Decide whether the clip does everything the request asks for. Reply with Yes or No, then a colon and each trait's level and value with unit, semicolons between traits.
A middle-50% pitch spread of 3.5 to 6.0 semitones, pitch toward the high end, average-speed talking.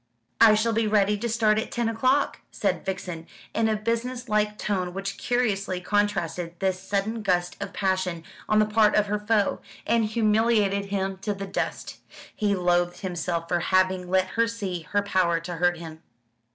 No: average, 3.0 semitones; high, 200 Hz; average, 180 wpm